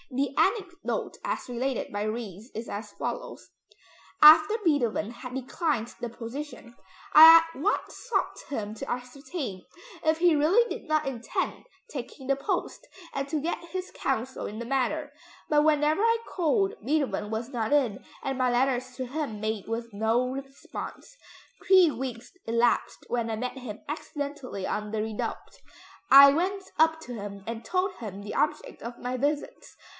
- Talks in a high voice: Yes, very high, 265 Hz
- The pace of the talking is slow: No, average, 160 wpm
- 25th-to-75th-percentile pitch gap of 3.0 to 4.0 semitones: No, average, 5.1 semitones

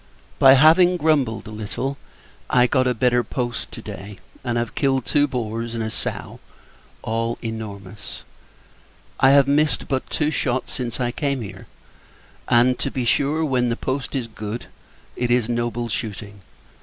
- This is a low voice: Yes, low, 125 Hz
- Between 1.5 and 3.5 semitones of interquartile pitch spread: Yes, average, 3.0 semitones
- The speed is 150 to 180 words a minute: Yes, average, 160 wpm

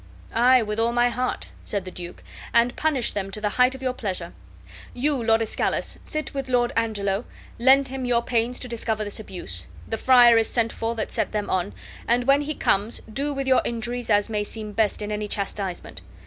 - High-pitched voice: Yes, high, 230 Hz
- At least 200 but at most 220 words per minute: Yes, fast, 205 wpm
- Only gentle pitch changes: No, average, 3.2 semitones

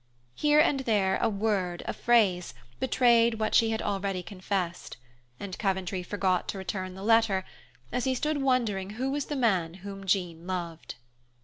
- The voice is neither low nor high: No, high, 200 Hz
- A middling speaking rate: Yes, average, 165 wpm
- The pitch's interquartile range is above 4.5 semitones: No, average, 3.9 semitones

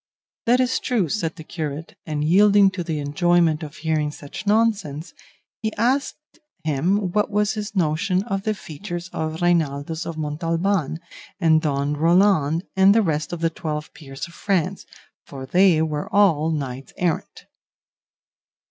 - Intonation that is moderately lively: Yes, average, 4.4 semitones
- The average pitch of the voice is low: No, medium, 165 Hz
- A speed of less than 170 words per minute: Yes, average, 150 wpm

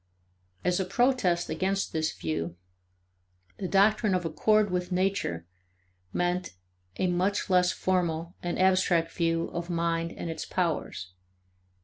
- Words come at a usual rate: No, slow, 125 wpm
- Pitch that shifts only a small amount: Yes, narrow, 2.2 semitones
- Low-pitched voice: No, medium, 180 Hz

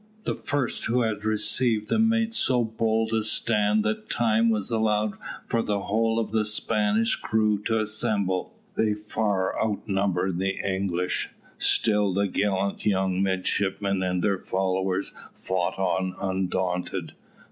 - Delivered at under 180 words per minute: Yes, slow, 135 wpm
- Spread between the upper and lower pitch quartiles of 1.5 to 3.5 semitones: Yes, average, 2.7 semitones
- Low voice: Yes, low, 105 Hz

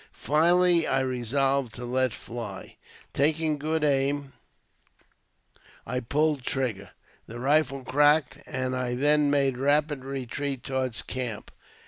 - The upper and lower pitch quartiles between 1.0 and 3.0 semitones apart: Yes, narrow, 2.6 semitones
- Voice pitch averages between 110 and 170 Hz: Yes, low, 135 Hz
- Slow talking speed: Yes, slow, 120 wpm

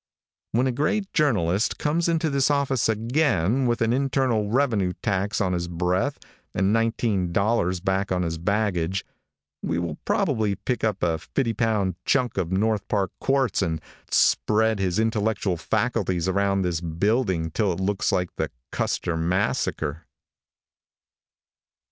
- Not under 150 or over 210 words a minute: No, average, 140 wpm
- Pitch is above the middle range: No, low, 100 Hz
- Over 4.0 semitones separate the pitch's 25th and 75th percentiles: Yes, average, 4.7 semitones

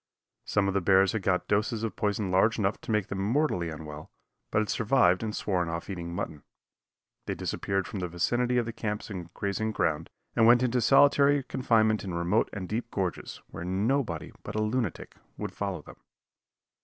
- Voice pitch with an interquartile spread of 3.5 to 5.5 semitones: Yes, average, 4.0 semitones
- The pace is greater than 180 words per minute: Yes, average, 190 wpm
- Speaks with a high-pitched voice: No, low, 105 Hz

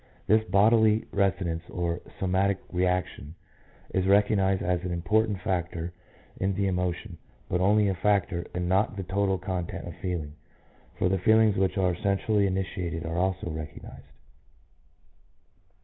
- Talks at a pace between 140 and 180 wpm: Yes, average, 150 wpm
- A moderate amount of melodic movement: No, narrow, 2.1 semitones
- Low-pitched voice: Yes, very low, 95 Hz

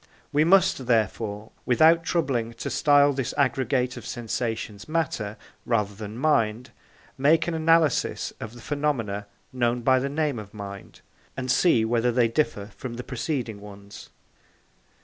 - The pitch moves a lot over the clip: No, average, 4.7 semitones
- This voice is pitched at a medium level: No, low, 125 Hz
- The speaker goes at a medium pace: Yes, average, 145 wpm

